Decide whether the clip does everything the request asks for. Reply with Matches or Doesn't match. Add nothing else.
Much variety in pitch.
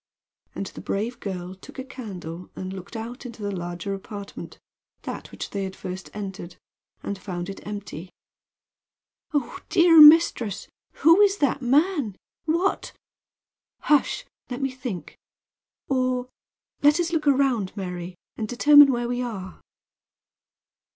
Matches